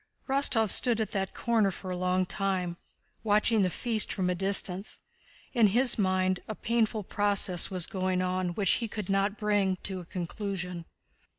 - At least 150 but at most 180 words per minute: Yes, average, 170 wpm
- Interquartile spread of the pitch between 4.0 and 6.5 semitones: No, average, 2.7 semitones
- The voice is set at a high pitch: Yes, high, 195 Hz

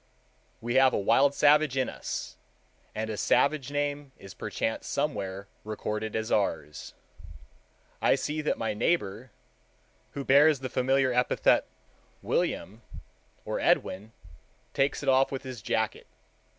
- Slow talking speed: Yes, slow, 130 wpm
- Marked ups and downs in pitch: No, average, 4.7 semitones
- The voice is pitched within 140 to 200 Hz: No, low, 130 Hz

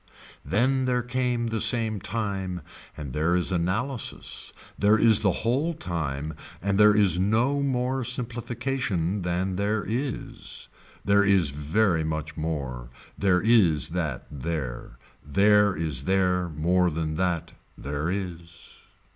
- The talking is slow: Yes, slow, 130 wpm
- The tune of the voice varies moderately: No, wide, 5.7 semitones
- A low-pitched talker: Yes, very low, 95 Hz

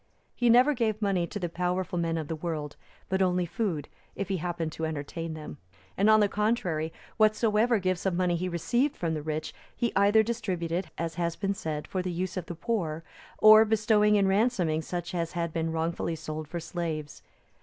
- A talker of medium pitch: Yes, medium, 180 Hz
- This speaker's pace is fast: No, average, 195 wpm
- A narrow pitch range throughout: No, average, 4.3 semitones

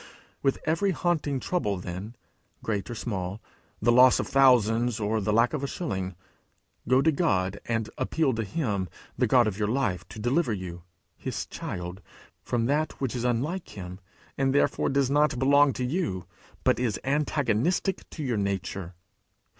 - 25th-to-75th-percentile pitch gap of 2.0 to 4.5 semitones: No, wide, 5.6 semitones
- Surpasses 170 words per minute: No, average, 160 wpm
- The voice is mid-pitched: No, low, 120 Hz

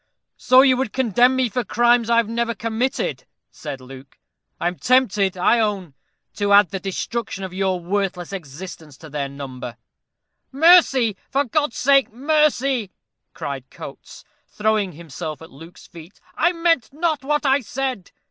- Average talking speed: Yes, average, 155 wpm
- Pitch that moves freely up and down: Yes, wide, 6.8 semitones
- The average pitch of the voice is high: Yes, high, 215 Hz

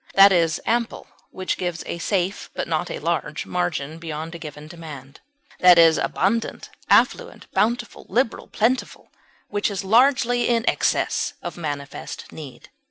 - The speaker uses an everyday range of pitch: No, wide, 6.1 semitones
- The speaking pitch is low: No, medium, 180 Hz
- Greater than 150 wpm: No, average, 145 wpm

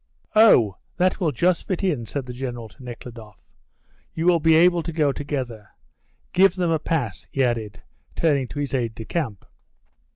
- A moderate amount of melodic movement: No, wide, 6.0 semitones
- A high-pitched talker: No, medium, 140 Hz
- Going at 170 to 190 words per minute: Yes, average, 175 wpm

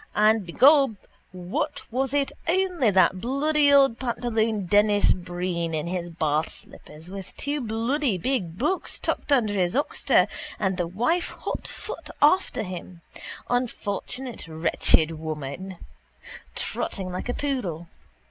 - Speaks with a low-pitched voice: No, high, 210 Hz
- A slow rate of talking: Yes, slow, 120 wpm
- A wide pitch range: Yes, wide, 7.1 semitones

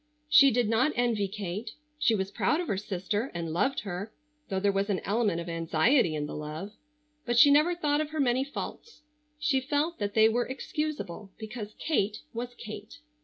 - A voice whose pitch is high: Yes, high, 220 Hz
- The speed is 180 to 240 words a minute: Yes, average, 190 wpm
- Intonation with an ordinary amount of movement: No, wide, 5.8 semitones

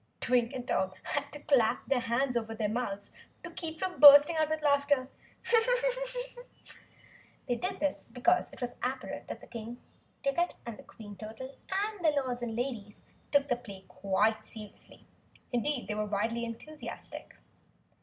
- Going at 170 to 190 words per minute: No, average, 150 wpm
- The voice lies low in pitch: No, very high, 250 Hz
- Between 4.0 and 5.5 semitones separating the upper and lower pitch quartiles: Yes, average, 4.6 semitones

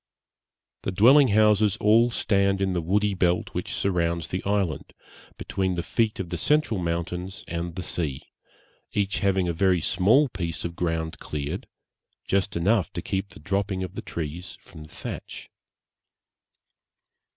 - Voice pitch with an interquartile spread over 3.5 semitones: No, average, 2.9 semitones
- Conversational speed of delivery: Yes, average, 150 wpm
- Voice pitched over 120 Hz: No, very low, 95 Hz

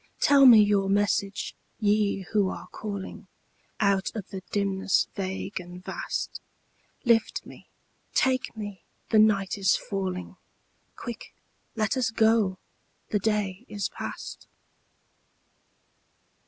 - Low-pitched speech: No, high, 205 Hz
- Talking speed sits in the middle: No, slow, 115 wpm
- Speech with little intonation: Yes, narrow, 2.2 semitones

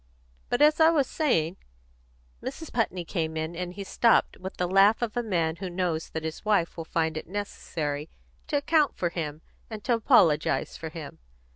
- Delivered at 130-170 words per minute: No, average, 185 wpm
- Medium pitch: Yes, medium, 175 Hz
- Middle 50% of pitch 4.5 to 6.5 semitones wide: Yes, wide, 5.5 semitones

